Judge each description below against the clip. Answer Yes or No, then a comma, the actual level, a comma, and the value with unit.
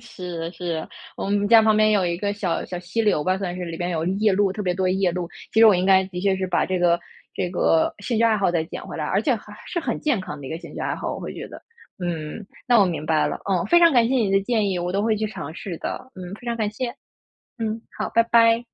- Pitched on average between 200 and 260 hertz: No, high, 190 Hz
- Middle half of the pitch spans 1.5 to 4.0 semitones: Yes, average, 3.7 semitones